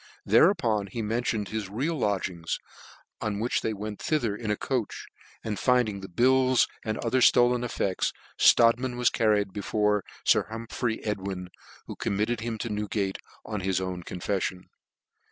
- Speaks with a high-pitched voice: No, low, 110 Hz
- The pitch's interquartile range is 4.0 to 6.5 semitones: No, average, 3.2 semitones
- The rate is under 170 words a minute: Yes, average, 155 wpm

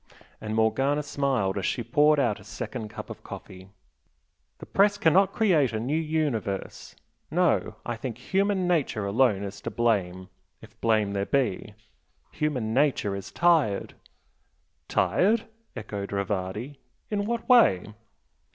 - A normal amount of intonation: No, wide, 7.1 semitones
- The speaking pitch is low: Yes, low, 120 Hz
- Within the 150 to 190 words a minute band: No, slow, 135 wpm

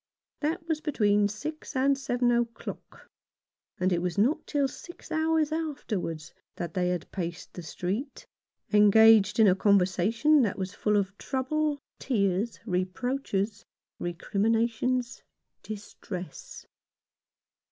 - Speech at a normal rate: No, slow, 115 wpm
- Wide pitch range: Yes, wide, 6.2 semitones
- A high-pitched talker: Yes, high, 220 Hz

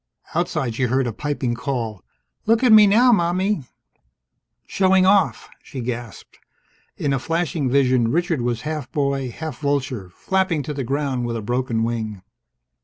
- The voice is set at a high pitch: No, medium, 140 Hz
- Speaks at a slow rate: No, average, 155 wpm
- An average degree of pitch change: No, wide, 5.8 semitones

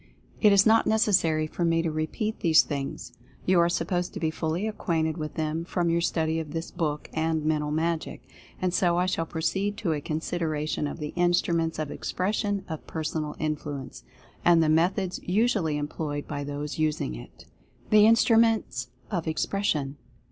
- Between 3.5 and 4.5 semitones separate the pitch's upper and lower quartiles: No, average, 2.9 semitones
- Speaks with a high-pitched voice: No, medium, 165 Hz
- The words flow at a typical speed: Yes, average, 170 wpm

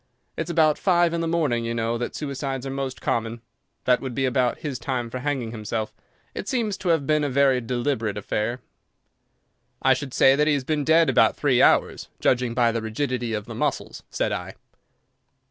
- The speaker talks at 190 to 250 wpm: Yes, average, 195 wpm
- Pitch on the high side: No, low, 130 Hz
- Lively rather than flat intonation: No, average, 4.0 semitones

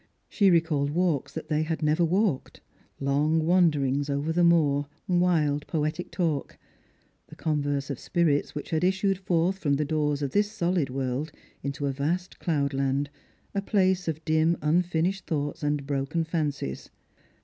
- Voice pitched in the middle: Yes, medium, 155 Hz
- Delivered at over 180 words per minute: No, average, 150 wpm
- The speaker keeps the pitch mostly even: No, average, 3.4 semitones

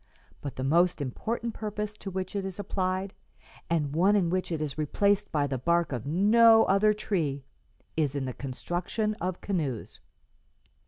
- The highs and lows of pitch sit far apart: Yes, wide, 5.7 semitones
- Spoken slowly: No, average, 165 wpm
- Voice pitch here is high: No, medium, 180 Hz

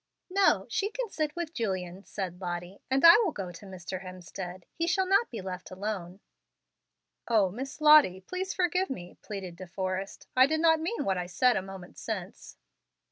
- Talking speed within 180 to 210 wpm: Yes, average, 185 wpm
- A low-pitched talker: No, high, 200 Hz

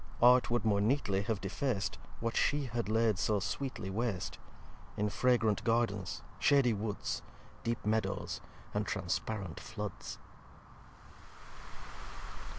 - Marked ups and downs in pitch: No, average, 3.0 semitones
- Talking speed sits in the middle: No, slow, 110 wpm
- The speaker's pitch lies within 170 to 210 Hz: No, low, 110 Hz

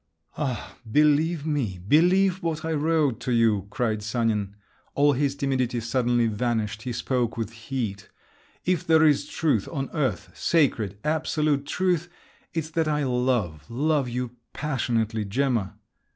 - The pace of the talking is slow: Yes, slow, 130 wpm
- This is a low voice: Yes, low, 130 Hz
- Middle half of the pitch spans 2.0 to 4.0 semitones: No, average, 5.1 semitones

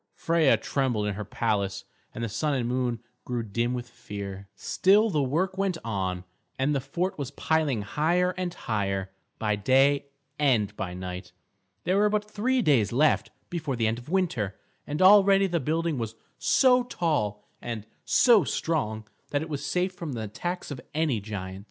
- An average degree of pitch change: No, wide, 8.1 semitones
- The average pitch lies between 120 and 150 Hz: Yes, low, 135 Hz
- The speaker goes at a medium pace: Yes, average, 175 wpm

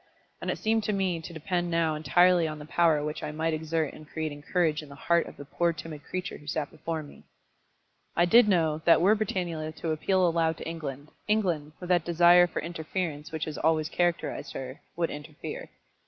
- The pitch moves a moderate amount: No, narrow, 2.2 semitones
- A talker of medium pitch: Yes, medium, 165 Hz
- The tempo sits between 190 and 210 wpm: Yes, fast, 205 wpm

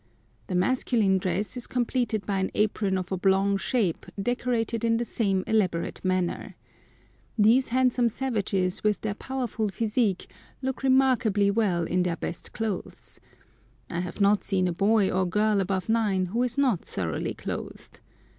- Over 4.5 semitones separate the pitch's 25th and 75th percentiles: No, average, 3.7 semitones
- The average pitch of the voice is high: Yes, high, 210 Hz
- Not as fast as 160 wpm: Yes, average, 150 wpm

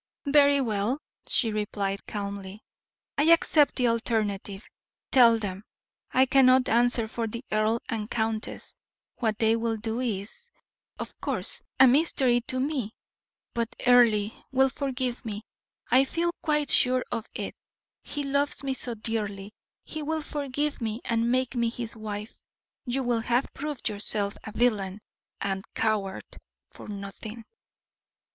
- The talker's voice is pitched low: No, high, 230 Hz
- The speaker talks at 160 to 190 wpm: No, average, 140 wpm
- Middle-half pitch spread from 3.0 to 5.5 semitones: Yes, average, 3.6 semitones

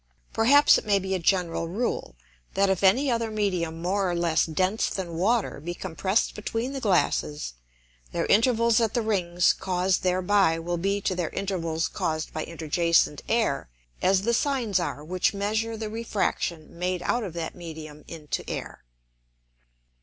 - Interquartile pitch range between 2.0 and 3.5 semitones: No, average, 4.3 semitones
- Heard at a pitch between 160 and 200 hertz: Yes, medium, 185 Hz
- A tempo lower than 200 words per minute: Yes, average, 160 wpm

